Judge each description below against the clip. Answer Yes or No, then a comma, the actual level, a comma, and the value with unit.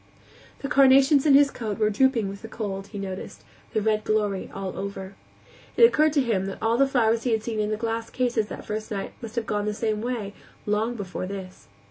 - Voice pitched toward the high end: Yes, high, 220 Hz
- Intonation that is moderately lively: Yes, average, 3.2 semitones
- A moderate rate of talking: No, fast, 220 wpm